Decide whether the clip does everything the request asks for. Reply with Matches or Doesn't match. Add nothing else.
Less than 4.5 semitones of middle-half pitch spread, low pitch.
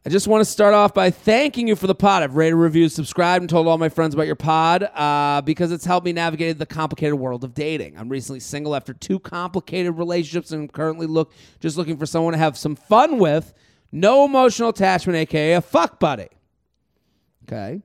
Doesn't match